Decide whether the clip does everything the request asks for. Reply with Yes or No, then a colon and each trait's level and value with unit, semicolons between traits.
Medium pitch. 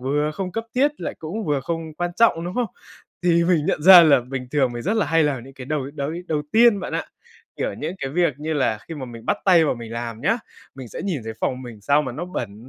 Yes: medium, 150 Hz